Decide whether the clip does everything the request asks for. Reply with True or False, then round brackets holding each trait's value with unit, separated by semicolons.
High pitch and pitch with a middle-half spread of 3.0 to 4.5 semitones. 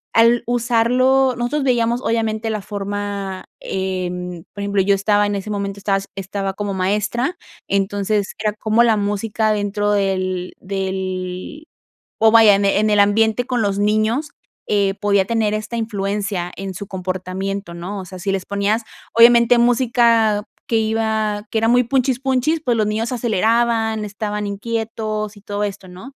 False (210 Hz; 2.5 semitones)